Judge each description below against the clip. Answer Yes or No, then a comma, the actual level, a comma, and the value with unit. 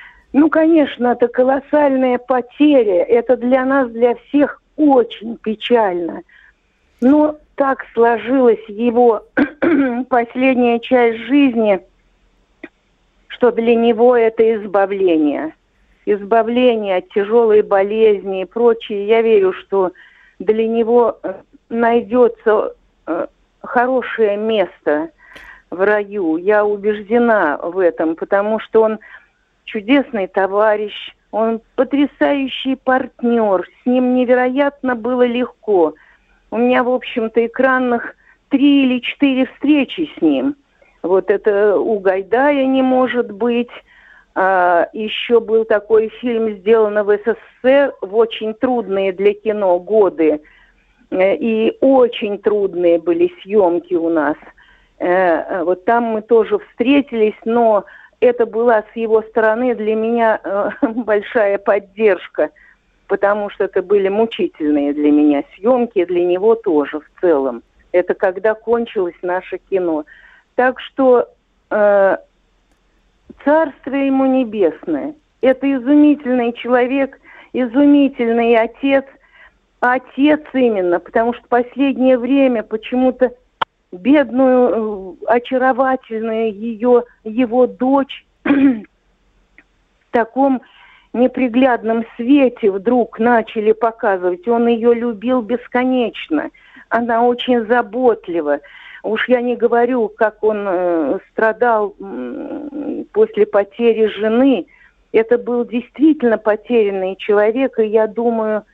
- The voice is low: No, high, 235 Hz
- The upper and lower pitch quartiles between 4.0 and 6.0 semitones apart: No, average, 3.5 semitones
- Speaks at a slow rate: Yes, slow, 100 wpm